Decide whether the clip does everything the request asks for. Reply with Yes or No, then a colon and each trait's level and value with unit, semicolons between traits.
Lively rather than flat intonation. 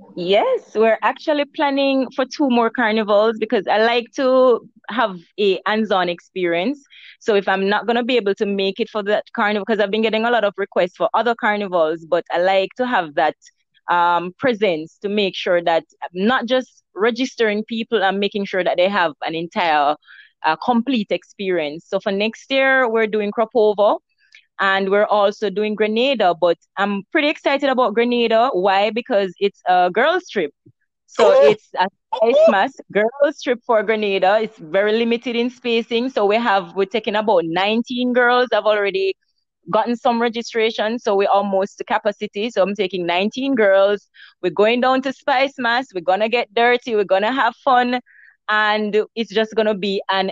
No: average, 3.7 semitones